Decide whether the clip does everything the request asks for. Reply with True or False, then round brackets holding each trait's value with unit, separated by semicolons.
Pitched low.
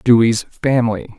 True (115 Hz)